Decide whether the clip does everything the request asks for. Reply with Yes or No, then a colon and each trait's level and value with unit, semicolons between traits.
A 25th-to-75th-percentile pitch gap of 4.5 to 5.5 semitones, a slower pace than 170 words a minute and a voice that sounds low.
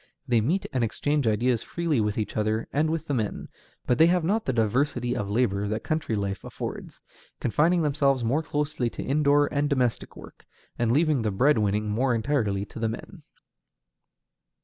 No: average, 5.2 semitones; average, 180 wpm; low, 125 Hz